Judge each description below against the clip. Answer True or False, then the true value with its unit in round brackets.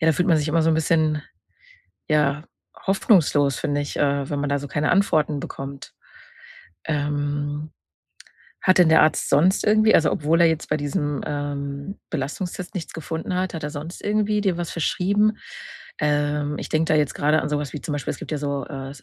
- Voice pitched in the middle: True (150 Hz)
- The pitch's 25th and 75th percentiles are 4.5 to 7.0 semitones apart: False (2.6 semitones)